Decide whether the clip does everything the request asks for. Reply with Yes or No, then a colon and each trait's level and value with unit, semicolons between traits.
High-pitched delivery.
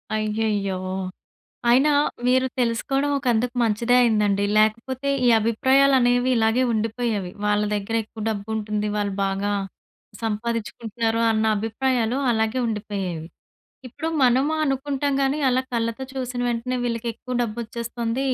Yes: high, 230 Hz